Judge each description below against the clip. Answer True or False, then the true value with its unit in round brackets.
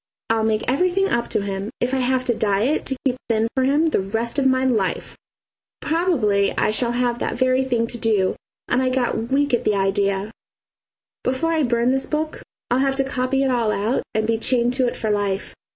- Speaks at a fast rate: True (215 wpm)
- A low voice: False (245 Hz)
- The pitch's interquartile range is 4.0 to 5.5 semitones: False (3.5 semitones)